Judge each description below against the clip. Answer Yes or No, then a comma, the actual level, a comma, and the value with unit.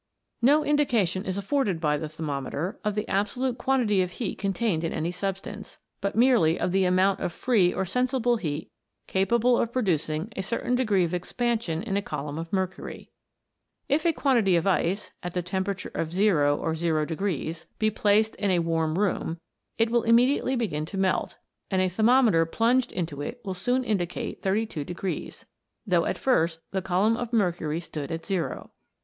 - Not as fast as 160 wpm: No, average, 175 wpm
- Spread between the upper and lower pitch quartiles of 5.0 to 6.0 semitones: Yes, wide, 5.4 semitones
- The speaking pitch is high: Yes, high, 195 Hz